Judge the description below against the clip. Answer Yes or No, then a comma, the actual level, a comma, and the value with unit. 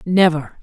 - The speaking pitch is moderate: Yes, medium, 165 Hz